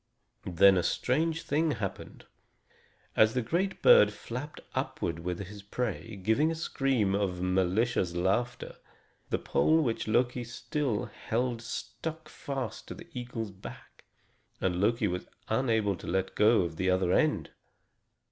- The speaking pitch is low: Yes, low, 110 Hz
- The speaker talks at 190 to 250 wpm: No, average, 140 wpm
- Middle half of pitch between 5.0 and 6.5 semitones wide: Yes, average, 5.3 semitones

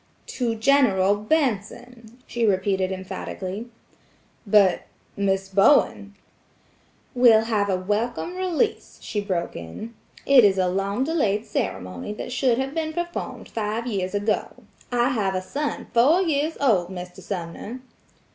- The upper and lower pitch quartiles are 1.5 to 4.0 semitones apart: No, average, 4.7 semitones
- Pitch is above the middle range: Yes, high, 215 Hz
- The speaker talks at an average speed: No, slow, 130 wpm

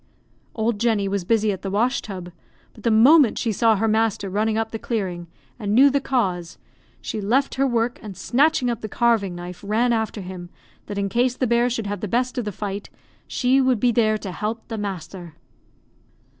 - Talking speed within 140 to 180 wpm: No, fast, 205 wpm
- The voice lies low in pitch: No, high, 220 Hz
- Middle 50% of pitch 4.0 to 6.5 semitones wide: No, average, 3.2 semitones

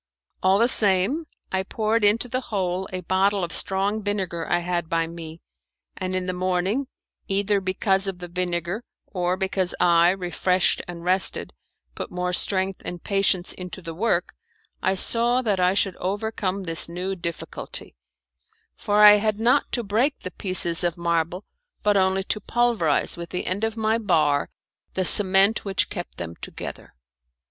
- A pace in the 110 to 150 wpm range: No, average, 165 wpm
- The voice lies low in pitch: No, high, 190 Hz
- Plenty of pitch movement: No, narrow, 2.6 semitones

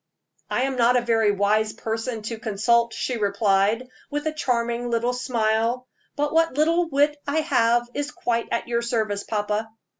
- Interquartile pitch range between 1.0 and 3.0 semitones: Yes, average, 2.7 semitones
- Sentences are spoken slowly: No, average, 170 wpm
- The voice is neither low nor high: No, high, 235 Hz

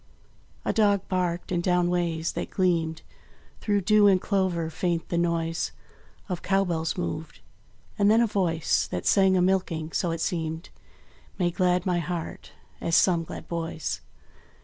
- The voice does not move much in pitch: Yes, narrow, 2.3 semitones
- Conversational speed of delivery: Yes, average, 155 wpm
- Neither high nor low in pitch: Yes, medium, 175 Hz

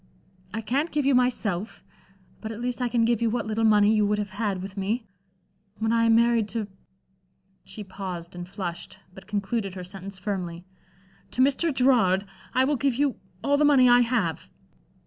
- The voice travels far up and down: No, average, 4.1 semitones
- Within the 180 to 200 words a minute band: Yes, average, 185 wpm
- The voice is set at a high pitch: Yes, high, 220 Hz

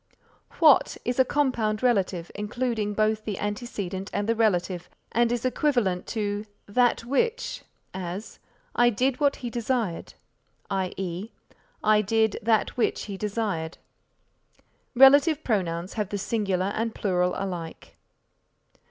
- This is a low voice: No, high, 215 Hz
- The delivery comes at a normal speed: No, slow, 125 wpm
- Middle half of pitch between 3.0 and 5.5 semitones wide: Yes, average, 3.9 semitones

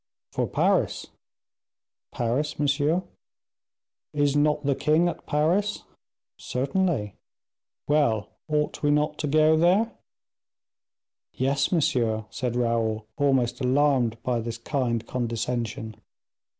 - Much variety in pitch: No, average, 4.3 semitones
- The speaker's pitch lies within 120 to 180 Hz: Yes, medium, 140 Hz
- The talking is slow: Yes, slow, 100 wpm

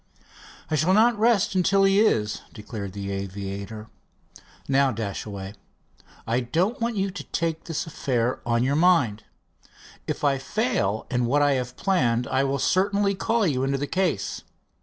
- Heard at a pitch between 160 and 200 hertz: No, low, 135 Hz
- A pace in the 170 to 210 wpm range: No, average, 160 wpm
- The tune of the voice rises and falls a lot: Yes, wide, 8.8 semitones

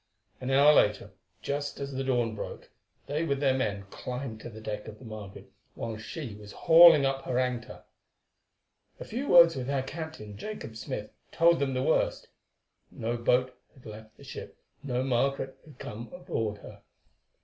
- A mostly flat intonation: No, average, 4.2 semitones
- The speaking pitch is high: No, low, 130 Hz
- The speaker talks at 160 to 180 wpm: Yes, average, 170 wpm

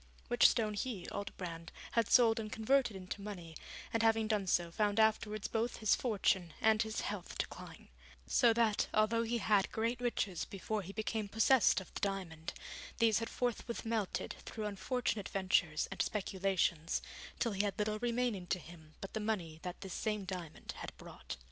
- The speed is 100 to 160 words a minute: No, average, 175 wpm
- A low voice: No, high, 210 Hz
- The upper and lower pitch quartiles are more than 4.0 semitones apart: No, average, 3.1 semitones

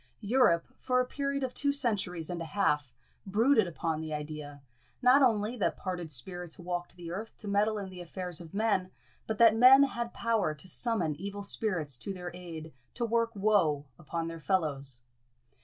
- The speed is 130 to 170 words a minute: No, average, 180 wpm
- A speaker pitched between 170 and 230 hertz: Yes, medium, 185 Hz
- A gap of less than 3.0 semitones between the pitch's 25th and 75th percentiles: No, wide, 5.5 semitones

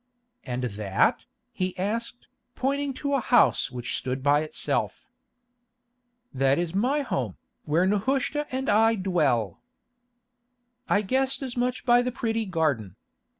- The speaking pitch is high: Yes, high, 200 Hz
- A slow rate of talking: Yes, slow, 130 wpm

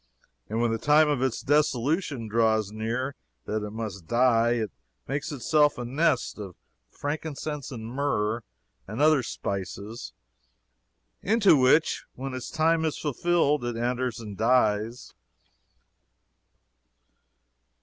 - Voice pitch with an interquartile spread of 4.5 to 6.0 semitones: Yes, average, 4.8 semitones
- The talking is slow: Yes, slow, 120 wpm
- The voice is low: Yes, low, 125 Hz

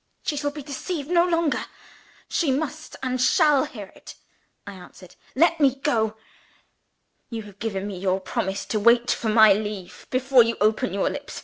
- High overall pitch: Yes, high, 235 Hz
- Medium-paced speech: Yes, average, 175 wpm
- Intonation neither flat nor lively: No, wide, 5.9 semitones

